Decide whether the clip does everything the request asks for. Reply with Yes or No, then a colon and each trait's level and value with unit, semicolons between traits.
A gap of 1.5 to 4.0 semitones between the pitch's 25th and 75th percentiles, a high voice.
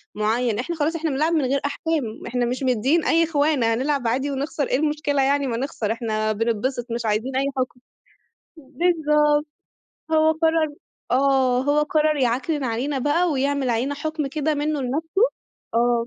Yes: average, 3.7 semitones; very high, 275 Hz